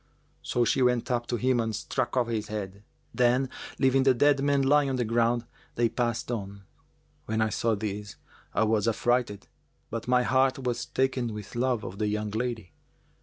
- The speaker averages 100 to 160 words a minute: No, average, 185 wpm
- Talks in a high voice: No, low, 120 Hz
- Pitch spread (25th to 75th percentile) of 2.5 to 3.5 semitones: Yes, average, 2.8 semitones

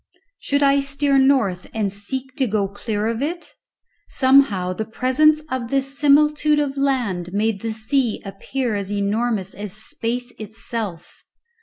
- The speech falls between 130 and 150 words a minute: Yes, average, 145 wpm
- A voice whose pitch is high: Yes, high, 235 Hz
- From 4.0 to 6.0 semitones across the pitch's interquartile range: Yes, average, 5.1 semitones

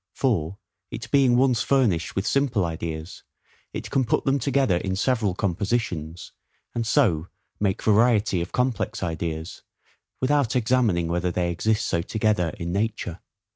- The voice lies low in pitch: Yes, low, 105 Hz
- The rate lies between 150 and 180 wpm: No, average, 140 wpm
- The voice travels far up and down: Yes, wide, 5.9 semitones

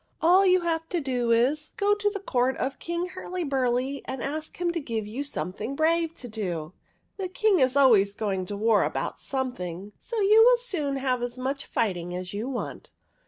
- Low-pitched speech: No, very high, 270 Hz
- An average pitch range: No, wide, 7.3 semitones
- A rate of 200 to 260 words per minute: Yes, fast, 205 wpm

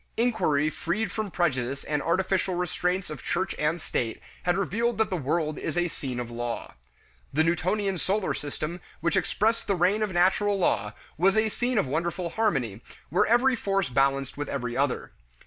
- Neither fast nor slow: Yes, average, 175 wpm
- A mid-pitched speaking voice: Yes, medium, 175 Hz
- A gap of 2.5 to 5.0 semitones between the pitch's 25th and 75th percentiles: No, wide, 5.6 semitones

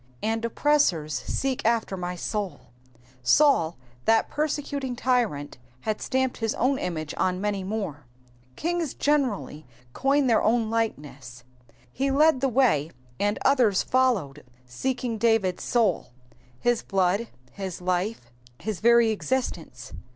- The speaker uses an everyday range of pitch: No, wide, 6.3 semitones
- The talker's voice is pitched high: Yes, high, 220 Hz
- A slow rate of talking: Yes, slow, 130 wpm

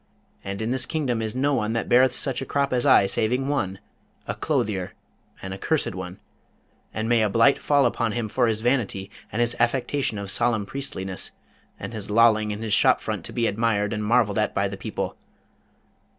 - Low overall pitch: Yes, low, 115 Hz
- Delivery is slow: No, average, 195 wpm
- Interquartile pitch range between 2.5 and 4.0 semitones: Yes, average, 3.3 semitones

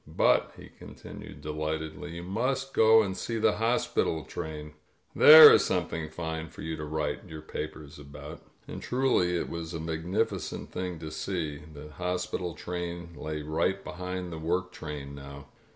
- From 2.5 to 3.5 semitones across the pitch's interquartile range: Yes, average, 2.9 semitones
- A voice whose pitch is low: Yes, very low, 80 Hz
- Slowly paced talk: No, average, 170 wpm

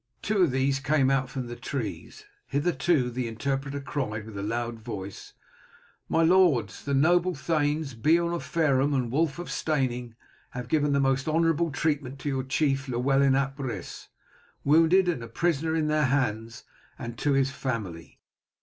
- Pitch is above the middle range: No, low, 135 Hz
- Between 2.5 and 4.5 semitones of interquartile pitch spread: Yes, average, 4.0 semitones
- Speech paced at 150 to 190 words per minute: Yes, average, 165 wpm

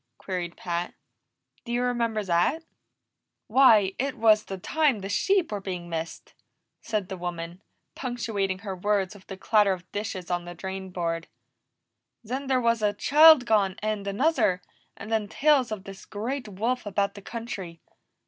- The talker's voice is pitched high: Yes, high, 205 Hz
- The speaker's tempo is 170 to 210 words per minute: No, average, 160 wpm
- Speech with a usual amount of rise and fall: Yes, average, 4.1 semitones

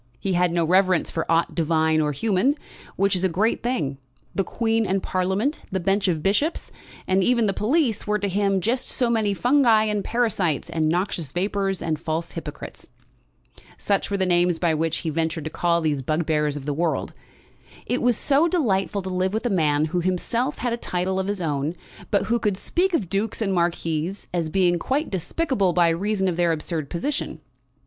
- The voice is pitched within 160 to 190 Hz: Yes, medium, 185 Hz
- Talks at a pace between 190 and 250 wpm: Yes, average, 195 wpm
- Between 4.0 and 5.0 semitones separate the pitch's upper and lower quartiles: Yes, average, 4.4 semitones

